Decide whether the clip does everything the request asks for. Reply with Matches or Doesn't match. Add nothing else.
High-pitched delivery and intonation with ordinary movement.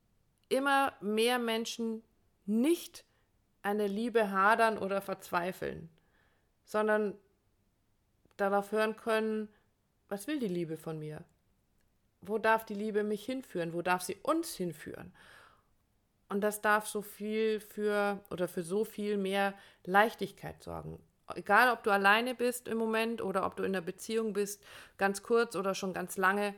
Matches